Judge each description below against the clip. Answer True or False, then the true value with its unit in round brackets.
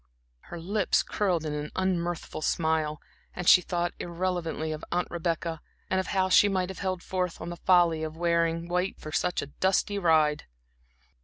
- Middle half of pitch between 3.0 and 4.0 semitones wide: False (2.4 semitones)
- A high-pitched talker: False (175 Hz)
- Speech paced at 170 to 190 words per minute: True (175 wpm)